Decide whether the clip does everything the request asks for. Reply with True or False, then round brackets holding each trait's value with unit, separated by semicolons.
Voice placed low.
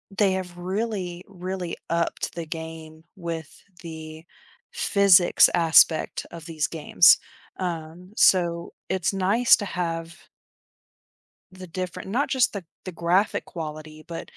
False (175 Hz)